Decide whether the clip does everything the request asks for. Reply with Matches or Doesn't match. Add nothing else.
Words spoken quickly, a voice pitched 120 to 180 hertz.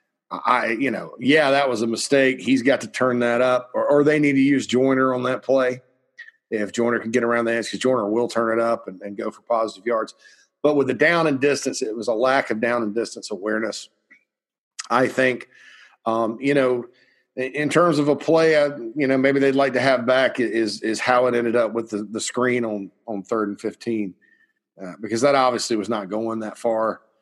Matches